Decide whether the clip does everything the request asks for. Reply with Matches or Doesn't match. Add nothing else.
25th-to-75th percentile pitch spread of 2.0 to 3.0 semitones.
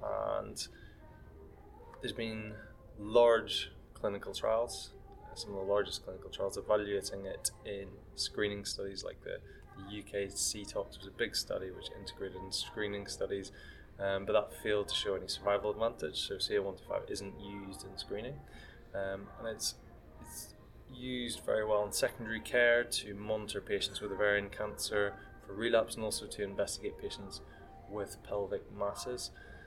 Matches